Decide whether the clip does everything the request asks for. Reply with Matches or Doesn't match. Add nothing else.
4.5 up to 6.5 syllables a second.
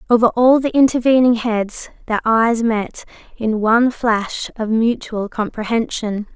Doesn't match